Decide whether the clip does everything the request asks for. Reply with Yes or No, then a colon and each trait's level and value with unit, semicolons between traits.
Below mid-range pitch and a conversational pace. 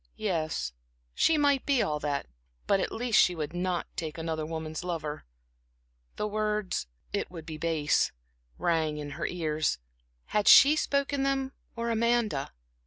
No: medium, 175 Hz; average, 150 wpm